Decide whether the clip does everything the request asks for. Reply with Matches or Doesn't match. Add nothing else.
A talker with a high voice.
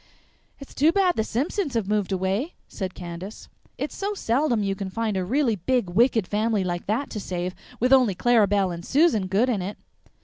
Matches